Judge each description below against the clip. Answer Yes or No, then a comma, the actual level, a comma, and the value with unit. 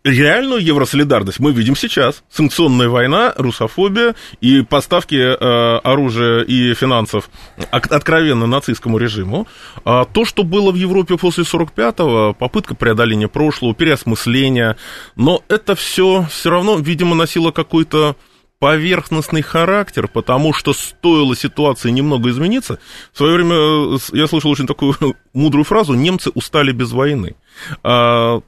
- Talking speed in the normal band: Yes, average, 120 wpm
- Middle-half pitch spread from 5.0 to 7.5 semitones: Yes, wide, 5.4 semitones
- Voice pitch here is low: No, medium, 145 Hz